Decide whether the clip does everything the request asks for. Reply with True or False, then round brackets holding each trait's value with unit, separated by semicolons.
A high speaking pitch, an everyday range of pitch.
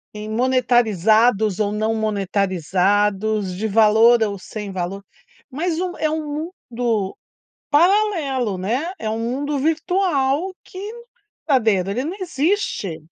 False (225 Hz; 6.4 semitones)